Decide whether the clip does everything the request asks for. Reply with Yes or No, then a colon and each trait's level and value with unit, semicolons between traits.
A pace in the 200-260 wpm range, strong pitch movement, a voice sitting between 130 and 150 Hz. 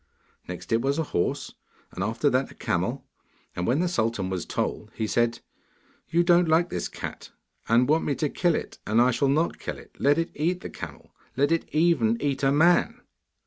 Yes: fast, 205 wpm; wide, 6.0 semitones; medium, 140 Hz